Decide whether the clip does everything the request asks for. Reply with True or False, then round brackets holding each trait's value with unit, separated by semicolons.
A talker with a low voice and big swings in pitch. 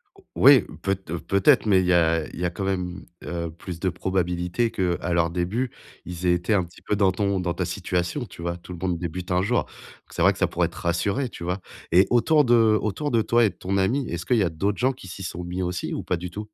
False (90 Hz; 2.7 semitones)